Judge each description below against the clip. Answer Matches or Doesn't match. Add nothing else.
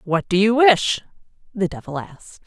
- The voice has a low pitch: Doesn't match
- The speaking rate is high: Doesn't match